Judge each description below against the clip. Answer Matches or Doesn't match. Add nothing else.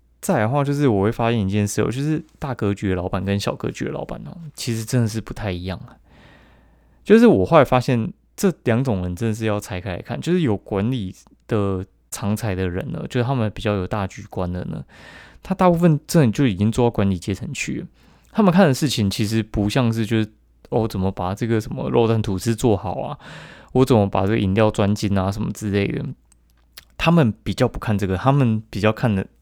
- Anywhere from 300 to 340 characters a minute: Matches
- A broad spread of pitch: Doesn't match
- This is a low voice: Matches